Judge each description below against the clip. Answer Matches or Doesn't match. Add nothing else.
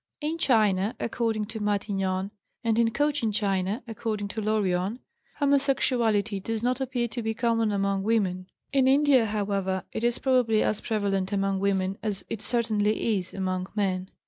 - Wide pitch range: Doesn't match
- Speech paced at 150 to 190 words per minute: Matches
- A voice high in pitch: Matches